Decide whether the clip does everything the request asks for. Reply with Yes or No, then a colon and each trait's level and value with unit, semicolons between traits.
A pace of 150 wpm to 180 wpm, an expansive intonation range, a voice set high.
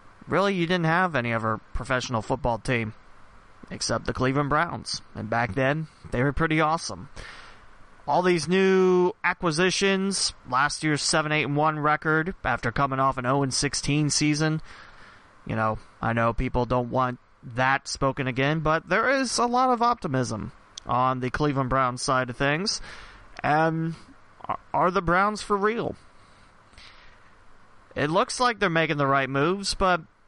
No: average, 155 wpm; wide, 5.7 semitones; medium, 145 Hz